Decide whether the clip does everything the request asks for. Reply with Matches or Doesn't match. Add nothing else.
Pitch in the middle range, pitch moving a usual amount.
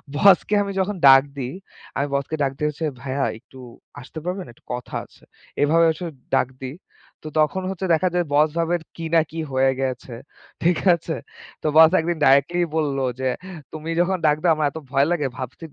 Matches